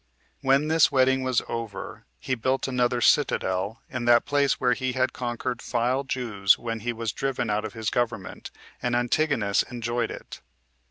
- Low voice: Yes, low, 120 Hz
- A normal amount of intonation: No, narrow, 2.2 semitones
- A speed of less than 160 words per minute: No, average, 170 wpm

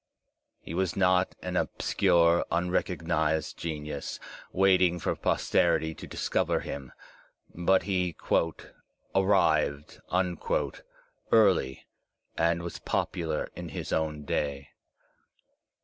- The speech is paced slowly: Yes, slow, 90 wpm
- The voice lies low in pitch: Yes, very low, 85 Hz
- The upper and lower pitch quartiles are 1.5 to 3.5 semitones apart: Yes, average, 2.9 semitones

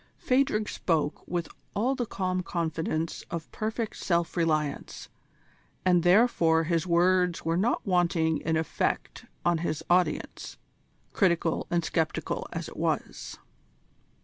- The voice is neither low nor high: Yes, medium, 170 Hz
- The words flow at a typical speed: No, slow, 120 wpm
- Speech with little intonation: Yes, narrow, 2.3 semitones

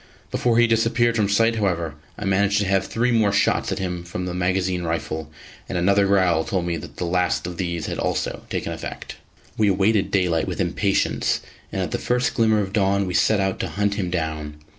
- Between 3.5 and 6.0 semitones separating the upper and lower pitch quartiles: No, average, 2.8 semitones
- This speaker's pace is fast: Yes, fast, 210 wpm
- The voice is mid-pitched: No, very low, 95 Hz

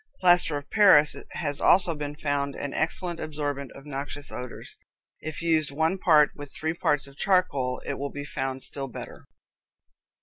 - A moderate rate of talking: Yes, average, 165 wpm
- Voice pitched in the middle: Yes, medium, 145 Hz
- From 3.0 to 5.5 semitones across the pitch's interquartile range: No, narrow, 2.4 semitones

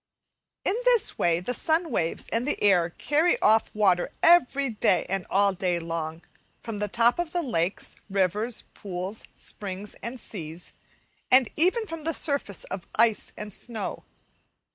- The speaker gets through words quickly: No, average, 145 wpm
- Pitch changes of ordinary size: No, wide, 7.3 semitones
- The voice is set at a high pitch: Yes, high, 210 Hz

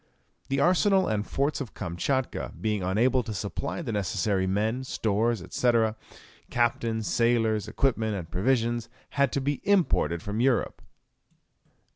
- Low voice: Yes, low, 115 Hz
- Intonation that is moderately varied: Yes, average, 4.2 semitones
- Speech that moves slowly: Yes, slow, 130 wpm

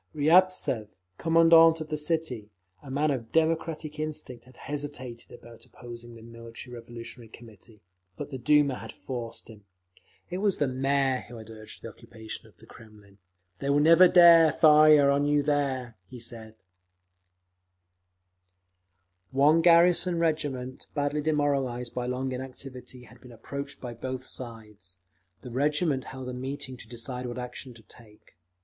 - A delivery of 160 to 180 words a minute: No, average, 150 wpm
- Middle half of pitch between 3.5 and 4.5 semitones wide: Yes, average, 4.2 semitones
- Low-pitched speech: Yes, low, 130 Hz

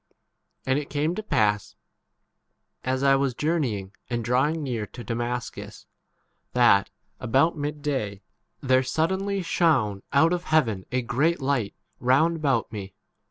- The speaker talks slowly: No, average, 155 wpm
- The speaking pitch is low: Yes, low, 130 Hz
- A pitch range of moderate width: Yes, average, 4.8 semitones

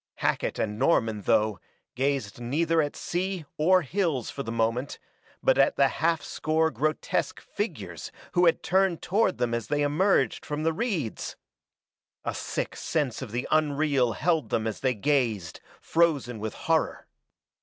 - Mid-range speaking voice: Yes, medium, 145 Hz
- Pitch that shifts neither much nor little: No, wide, 5.7 semitones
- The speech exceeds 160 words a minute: No, average, 155 wpm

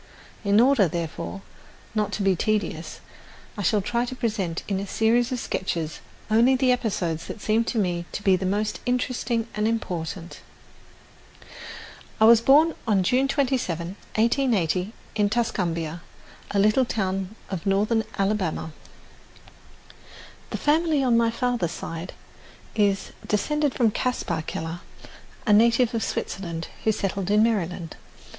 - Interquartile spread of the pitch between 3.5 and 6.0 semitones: Yes, average, 4.2 semitones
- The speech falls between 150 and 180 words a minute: No, slow, 135 wpm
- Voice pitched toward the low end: No, high, 210 Hz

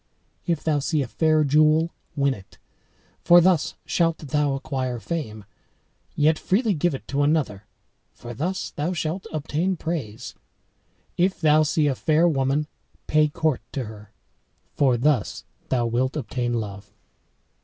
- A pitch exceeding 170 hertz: No, medium, 150 Hz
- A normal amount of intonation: Yes, average, 4.0 semitones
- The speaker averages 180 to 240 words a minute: No, average, 145 wpm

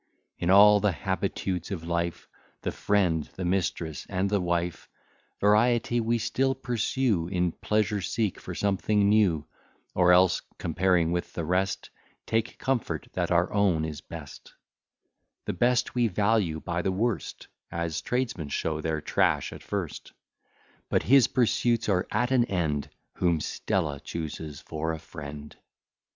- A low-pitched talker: Yes, very low, 95 Hz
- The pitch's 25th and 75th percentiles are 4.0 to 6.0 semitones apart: Yes, average, 4.5 semitones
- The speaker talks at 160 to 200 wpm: No, average, 145 wpm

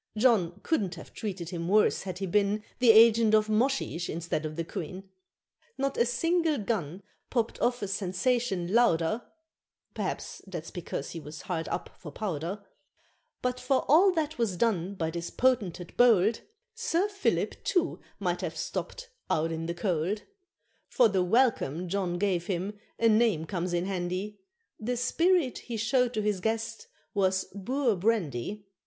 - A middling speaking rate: Yes, average, 160 wpm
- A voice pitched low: No, high, 205 Hz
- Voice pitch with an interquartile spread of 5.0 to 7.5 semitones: Yes, average, 5.3 semitones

